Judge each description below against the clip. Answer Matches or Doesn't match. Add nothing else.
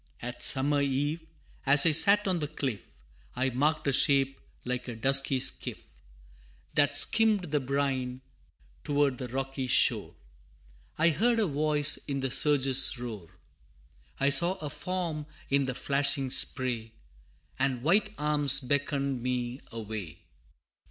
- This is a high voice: Doesn't match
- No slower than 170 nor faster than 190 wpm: Doesn't match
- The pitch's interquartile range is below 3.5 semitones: Matches